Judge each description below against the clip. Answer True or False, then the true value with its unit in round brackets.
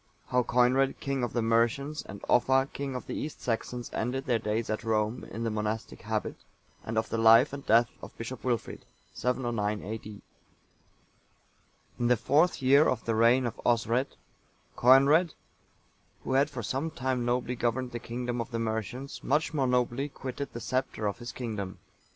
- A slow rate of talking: False (175 wpm)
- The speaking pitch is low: True (120 Hz)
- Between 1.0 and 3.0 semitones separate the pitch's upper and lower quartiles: True (2.7 semitones)